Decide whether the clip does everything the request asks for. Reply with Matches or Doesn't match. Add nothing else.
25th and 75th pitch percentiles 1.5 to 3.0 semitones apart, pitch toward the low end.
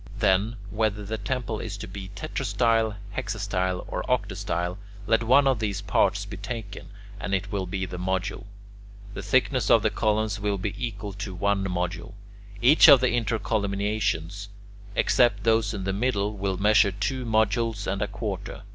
Matches